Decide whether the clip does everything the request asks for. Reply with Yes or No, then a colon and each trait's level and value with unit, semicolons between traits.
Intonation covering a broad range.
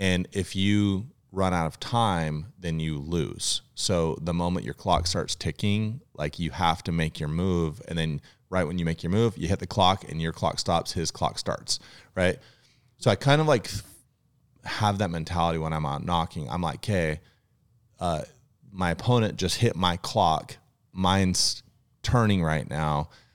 Yes: wide, 5.9 semitones